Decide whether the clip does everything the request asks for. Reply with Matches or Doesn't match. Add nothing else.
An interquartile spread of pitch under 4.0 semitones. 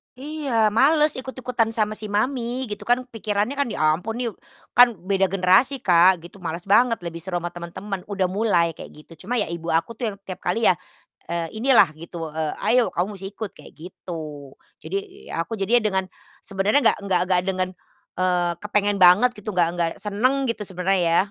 Doesn't match